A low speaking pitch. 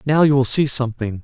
Yes: low, 130 Hz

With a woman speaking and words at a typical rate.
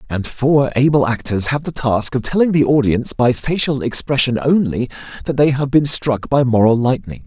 No: male; average, 190 wpm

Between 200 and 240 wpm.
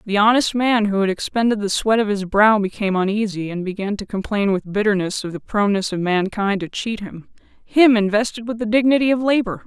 Yes: fast, 205 wpm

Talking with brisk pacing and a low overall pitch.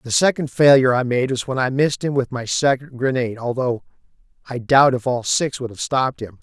Yes: fast, 225 wpm; low, 130 Hz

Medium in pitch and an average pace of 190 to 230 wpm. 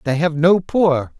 Yes: medium, 160 Hz; average, 200 wpm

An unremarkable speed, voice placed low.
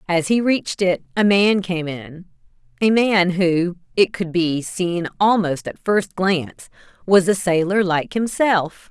No: average, 160 wpm; medium, 185 Hz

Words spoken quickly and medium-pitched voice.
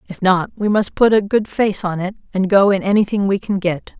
No: fast, 255 wpm; high, 195 Hz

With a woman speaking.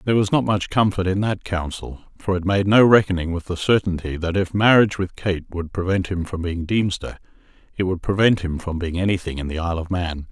No: male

